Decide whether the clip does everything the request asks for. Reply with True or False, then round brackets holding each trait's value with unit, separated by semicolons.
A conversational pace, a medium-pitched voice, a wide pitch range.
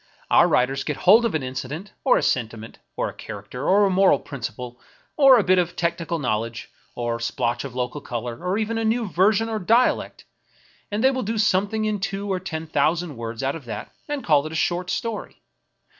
False (215 wpm; 170 Hz; 8.6 semitones)